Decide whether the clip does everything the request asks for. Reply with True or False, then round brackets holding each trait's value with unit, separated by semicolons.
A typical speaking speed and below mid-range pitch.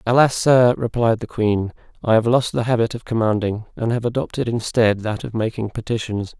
True (190 wpm; 115 Hz)